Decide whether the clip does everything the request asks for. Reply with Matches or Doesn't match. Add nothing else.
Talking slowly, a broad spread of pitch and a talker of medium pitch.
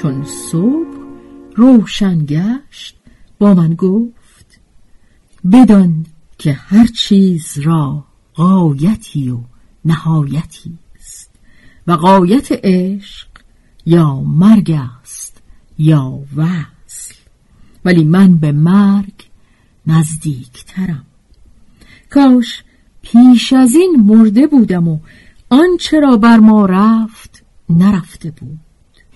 Matches